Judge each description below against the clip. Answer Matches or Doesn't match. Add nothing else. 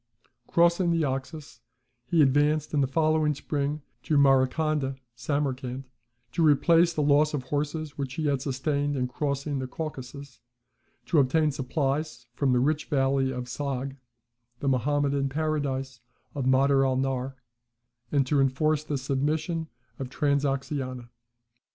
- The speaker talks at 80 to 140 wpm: Matches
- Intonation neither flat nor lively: Doesn't match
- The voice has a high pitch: Doesn't match